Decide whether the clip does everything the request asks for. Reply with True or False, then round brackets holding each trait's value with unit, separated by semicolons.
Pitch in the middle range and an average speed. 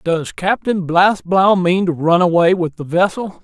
True (175 Hz; 175 wpm)